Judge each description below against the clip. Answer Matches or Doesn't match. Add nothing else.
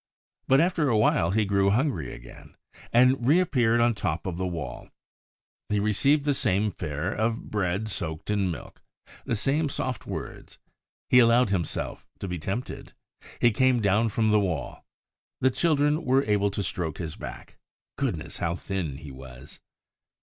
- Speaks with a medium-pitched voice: Doesn't match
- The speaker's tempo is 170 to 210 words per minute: Doesn't match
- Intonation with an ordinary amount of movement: Doesn't match